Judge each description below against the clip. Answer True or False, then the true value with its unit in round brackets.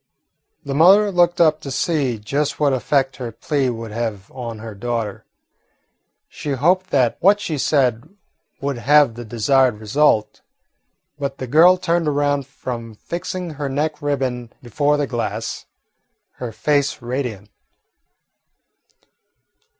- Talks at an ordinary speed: False (130 wpm)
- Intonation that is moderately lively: True (4.1 semitones)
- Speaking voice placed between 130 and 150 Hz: True (135 Hz)